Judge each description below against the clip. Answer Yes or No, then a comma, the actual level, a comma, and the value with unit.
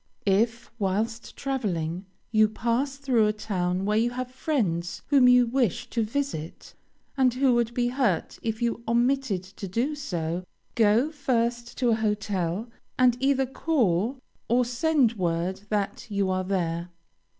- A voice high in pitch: Yes, high, 230 Hz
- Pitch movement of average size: Yes, average, 4.7 semitones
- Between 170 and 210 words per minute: No, average, 150 wpm